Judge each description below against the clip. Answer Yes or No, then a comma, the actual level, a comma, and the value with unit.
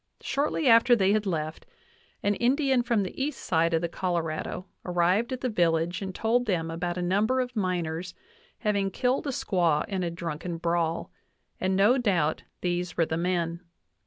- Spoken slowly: No, average, 175 wpm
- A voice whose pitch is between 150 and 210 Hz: Yes, medium, 185 Hz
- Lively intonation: No, average, 4.9 semitones